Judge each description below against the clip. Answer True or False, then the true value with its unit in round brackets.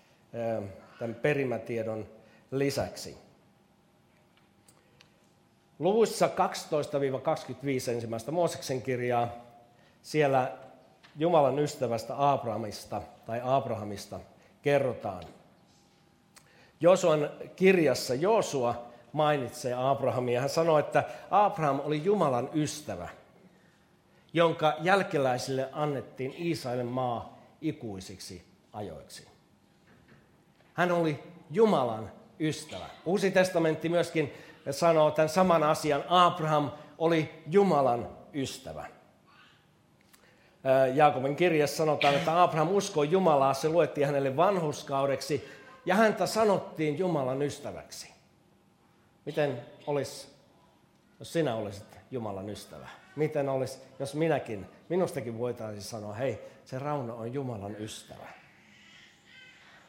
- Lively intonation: False (4.5 semitones)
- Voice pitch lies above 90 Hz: True (140 Hz)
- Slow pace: True (85 wpm)